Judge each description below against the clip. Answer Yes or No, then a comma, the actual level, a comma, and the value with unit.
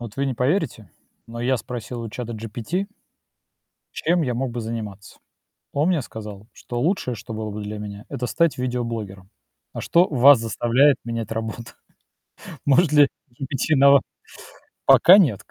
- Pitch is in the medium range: No, low, 120 Hz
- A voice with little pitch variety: No, average, 4.0 semitones